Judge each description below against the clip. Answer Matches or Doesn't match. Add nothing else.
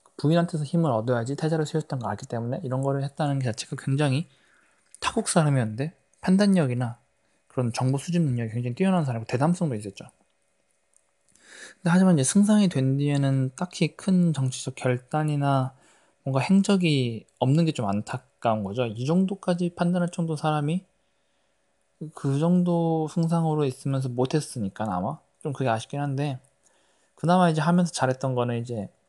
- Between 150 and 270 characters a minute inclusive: Doesn't match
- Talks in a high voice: Doesn't match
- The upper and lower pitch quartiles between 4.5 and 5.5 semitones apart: Matches